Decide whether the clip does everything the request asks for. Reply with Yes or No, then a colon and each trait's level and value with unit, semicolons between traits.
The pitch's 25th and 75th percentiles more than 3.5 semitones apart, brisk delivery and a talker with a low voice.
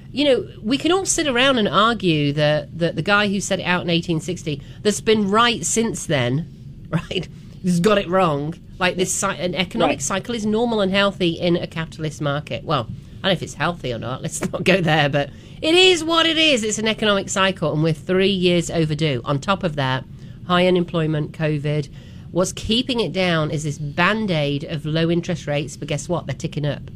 No: average, 4.7 semitones; fast, 210 wpm; medium, 175 Hz